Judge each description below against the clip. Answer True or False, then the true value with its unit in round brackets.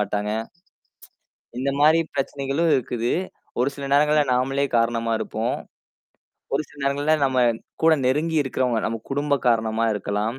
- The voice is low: True (130 Hz)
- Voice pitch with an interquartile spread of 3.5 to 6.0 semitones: True (3.8 semitones)